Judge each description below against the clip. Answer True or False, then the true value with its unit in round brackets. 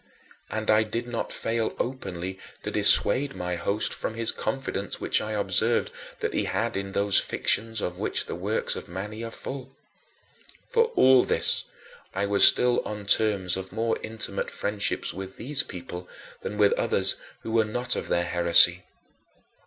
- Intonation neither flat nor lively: True (3.3 semitones)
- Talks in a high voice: False (105 Hz)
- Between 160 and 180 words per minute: True (165 wpm)